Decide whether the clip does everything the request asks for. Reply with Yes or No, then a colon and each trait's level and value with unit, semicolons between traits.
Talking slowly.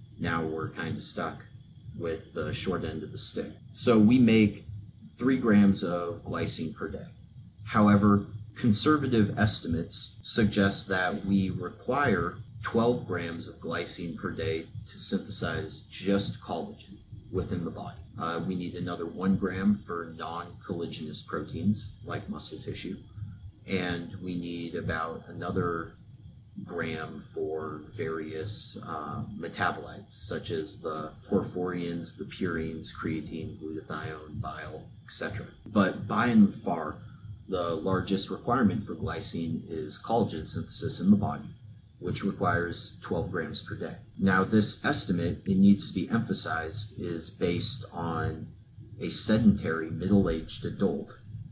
Yes: slow, 130 wpm